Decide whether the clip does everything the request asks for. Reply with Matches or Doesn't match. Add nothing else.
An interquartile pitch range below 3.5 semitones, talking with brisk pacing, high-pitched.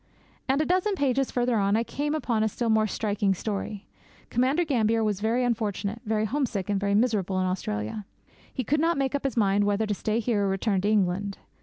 Doesn't match